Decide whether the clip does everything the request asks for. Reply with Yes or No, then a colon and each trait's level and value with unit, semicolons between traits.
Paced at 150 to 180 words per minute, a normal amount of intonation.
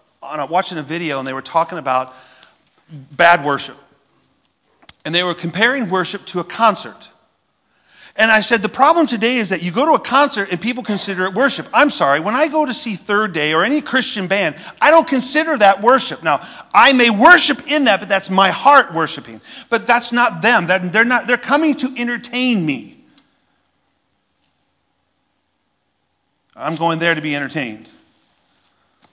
No: average, 175 wpm; wide, 6.8 semitones